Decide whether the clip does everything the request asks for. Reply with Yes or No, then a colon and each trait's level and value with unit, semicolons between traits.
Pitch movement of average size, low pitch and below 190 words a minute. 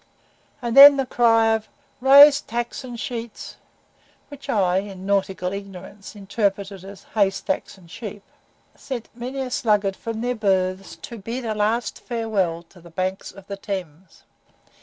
No: average, 3.6 semitones; high, 210 Hz; average, 150 wpm